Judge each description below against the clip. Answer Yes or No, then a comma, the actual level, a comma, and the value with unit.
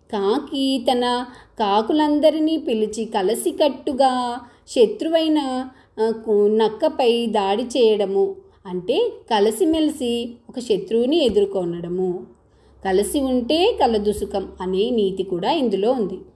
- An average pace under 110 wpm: Yes, average, 80 wpm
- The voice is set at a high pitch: Yes, high, 240 Hz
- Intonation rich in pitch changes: Yes, wide, 6.5 semitones